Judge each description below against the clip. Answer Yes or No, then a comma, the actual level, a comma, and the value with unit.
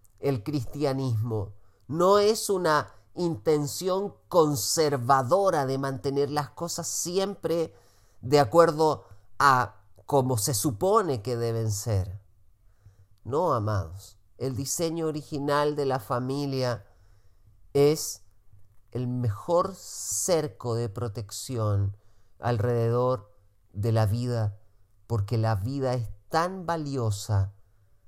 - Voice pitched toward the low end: Yes, low, 120 Hz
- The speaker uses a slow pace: Yes, slow, 95 wpm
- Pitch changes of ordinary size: No, wide, 6.2 semitones